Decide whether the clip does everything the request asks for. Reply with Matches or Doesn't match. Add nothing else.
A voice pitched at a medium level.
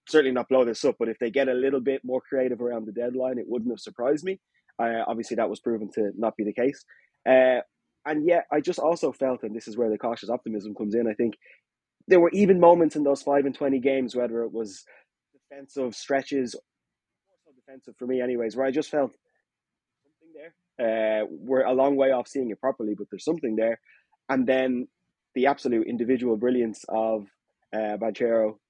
Doesn't match